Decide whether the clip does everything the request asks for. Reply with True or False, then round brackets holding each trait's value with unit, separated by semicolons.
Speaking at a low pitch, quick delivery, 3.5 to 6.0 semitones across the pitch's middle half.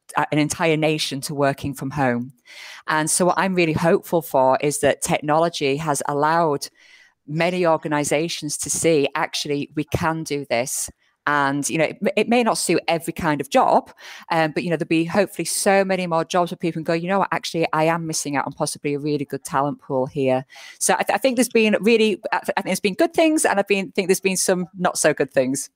False (160 Hz; 230 wpm; 3.8 semitones)